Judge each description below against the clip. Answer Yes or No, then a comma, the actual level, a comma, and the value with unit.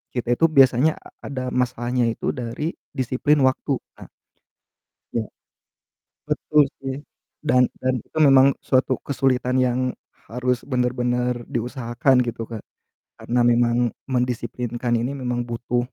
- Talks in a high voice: No, low, 125 Hz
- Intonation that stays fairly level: Yes, narrow, 1.5 semitones